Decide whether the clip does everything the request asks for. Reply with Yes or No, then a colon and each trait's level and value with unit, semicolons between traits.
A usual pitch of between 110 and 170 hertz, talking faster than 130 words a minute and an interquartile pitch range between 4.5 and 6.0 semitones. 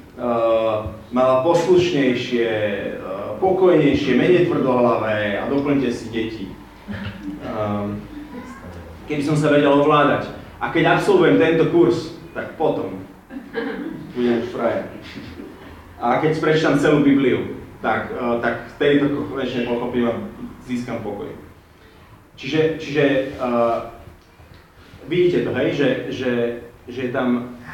No: low, 125 Hz; average, 115 wpm; wide, 5.4 semitones